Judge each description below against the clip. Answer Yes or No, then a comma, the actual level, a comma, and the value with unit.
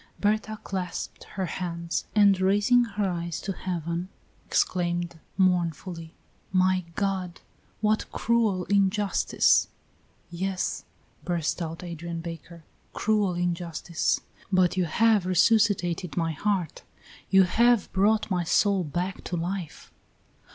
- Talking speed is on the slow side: Yes, slow, 110 wpm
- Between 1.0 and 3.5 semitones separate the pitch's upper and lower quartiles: Yes, average, 2.7 semitones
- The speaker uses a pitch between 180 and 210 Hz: Yes, medium, 185 Hz